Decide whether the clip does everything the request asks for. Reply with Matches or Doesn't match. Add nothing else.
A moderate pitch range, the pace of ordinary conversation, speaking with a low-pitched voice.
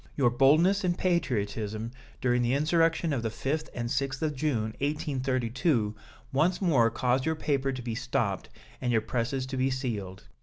Matches